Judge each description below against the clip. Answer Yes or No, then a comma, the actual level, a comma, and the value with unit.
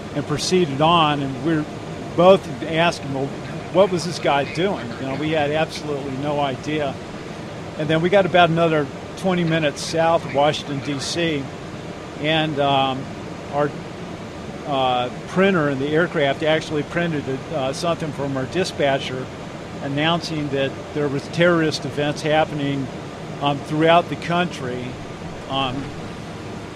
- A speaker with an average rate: No, slow, 130 wpm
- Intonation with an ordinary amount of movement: Yes, average, 3.2 semitones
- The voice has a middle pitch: Yes, medium, 150 Hz